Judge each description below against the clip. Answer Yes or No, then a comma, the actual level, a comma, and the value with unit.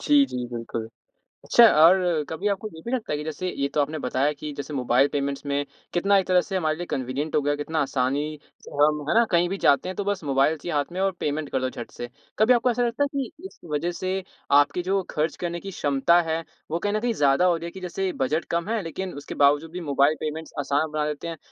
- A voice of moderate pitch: Yes, medium, 160 Hz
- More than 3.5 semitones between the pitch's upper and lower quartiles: Yes, average, 4.6 semitones